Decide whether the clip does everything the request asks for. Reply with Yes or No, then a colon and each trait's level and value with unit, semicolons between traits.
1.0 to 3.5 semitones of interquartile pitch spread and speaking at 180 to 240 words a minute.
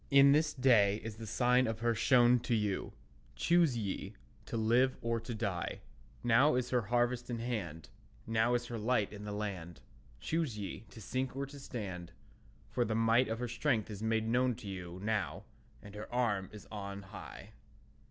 Yes: average, 3.1 semitones; average, 185 wpm